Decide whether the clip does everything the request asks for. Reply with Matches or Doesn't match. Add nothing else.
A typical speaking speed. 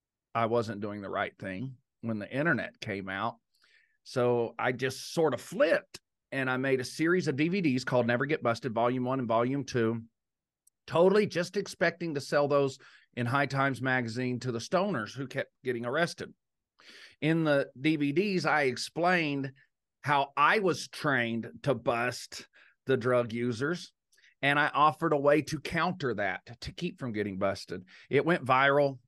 Matches